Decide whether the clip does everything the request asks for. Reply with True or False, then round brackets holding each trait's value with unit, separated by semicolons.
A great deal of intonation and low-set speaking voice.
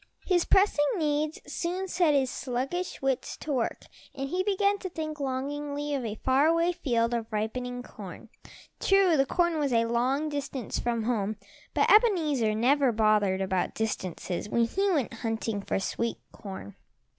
False (5.7 semitones; 270 Hz)